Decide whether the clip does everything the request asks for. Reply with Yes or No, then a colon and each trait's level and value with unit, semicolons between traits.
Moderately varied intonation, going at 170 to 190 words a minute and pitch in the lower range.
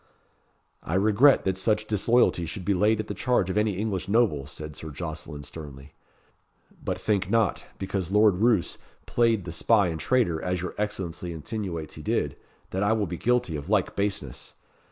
Yes: average, 4.6 semitones; average, 175 wpm; very low, 95 Hz